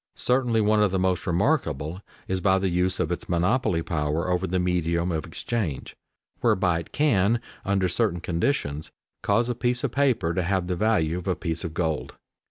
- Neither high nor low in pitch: No, very low, 90 Hz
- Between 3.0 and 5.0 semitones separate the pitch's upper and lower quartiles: Yes, average, 4.1 semitones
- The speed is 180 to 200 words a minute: Yes, average, 185 wpm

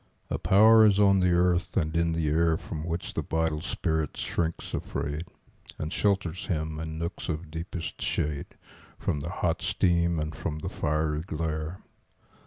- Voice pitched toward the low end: Yes, very low, 80 Hz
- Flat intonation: Yes, narrow, 2.1 semitones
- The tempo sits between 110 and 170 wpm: Yes, average, 165 wpm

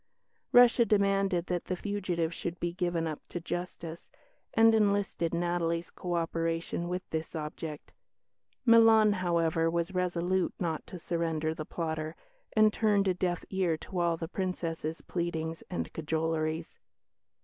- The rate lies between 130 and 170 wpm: Yes, average, 140 wpm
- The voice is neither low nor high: Yes, medium, 175 Hz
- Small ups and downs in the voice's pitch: Yes, narrow, 2.3 semitones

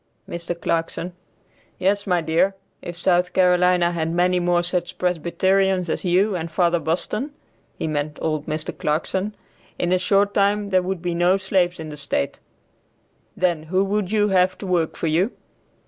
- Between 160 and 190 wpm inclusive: Yes, average, 165 wpm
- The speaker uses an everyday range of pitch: No, narrow, 2.1 semitones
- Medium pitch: Yes, medium, 180 Hz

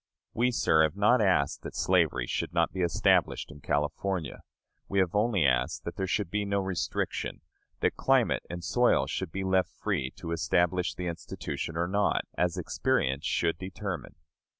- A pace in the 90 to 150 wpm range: No, average, 165 wpm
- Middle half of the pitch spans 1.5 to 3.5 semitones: Yes, average, 3.2 semitones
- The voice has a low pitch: Yes, very low, 90 Hz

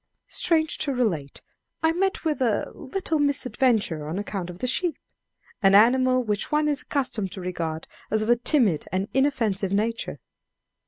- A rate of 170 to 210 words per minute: No, average, 160 wpm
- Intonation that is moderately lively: No, wide, 6.6 semitones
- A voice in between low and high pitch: No, high, 235 Hz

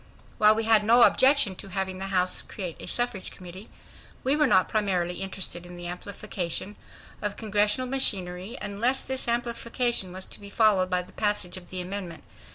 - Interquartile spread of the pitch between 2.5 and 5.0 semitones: Yes, average, 3.7 semitones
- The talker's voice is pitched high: Yes, high, 200 Hz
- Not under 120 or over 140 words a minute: No, average, 175 wpm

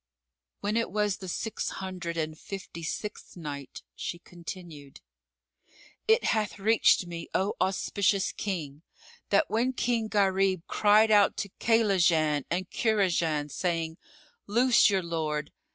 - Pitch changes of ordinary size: Yes, average, 4.1 semitones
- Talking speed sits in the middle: No, slow, 125 wpm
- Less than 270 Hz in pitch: Yes, high, 190 Hz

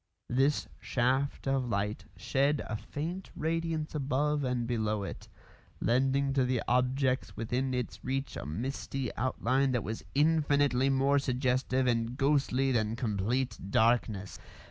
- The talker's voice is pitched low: Yes, low, 130 Hz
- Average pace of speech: No, slow, 130 wpm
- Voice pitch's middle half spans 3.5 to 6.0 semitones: No, average, 2.7 semitones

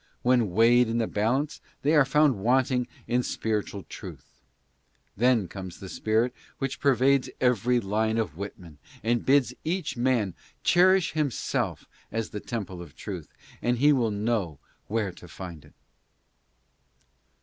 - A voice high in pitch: No, low, 115 Hz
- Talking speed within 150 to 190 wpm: No, average, 140 wpm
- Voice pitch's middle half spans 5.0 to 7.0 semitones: No, average, 4.1 semitones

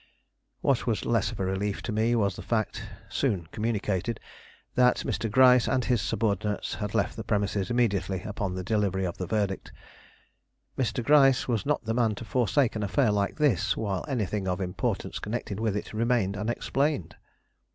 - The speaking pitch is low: Yes, low, 105 Hz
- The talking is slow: No, average, 170 wpm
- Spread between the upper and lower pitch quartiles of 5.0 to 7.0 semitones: No, average, 3.3 semitones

